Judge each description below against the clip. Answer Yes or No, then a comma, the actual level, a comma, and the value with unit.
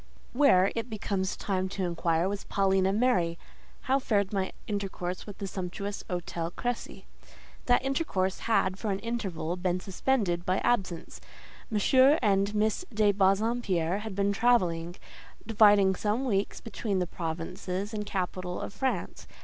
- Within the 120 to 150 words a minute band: Yes, average, 140 wpm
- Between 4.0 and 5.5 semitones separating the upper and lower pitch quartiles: No, average, 3.0 semitones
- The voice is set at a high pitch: Yes, high, 195 Hz